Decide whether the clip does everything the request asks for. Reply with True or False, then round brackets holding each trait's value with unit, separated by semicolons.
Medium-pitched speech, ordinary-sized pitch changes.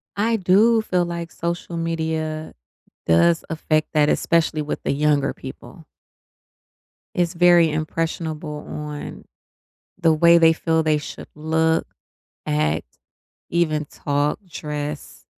False (160 Hz; 2.1 semitones)